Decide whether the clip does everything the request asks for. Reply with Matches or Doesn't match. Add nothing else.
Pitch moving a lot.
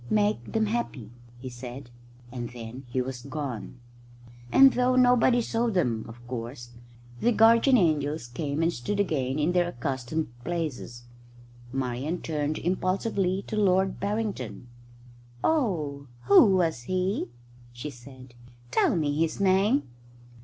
Matches